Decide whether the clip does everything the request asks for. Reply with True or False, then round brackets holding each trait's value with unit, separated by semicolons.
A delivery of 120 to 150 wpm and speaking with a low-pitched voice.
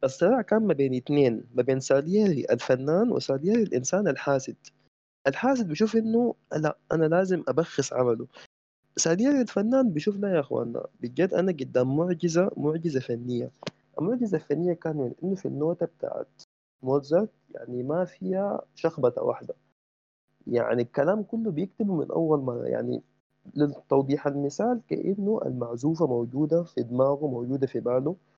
False (135 wpm; 160 Hz)